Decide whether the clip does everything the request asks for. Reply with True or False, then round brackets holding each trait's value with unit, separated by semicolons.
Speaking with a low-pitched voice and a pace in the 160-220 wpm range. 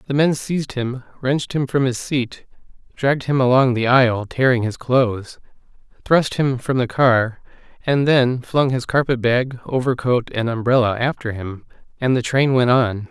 True (125 Hz; 175 wpm)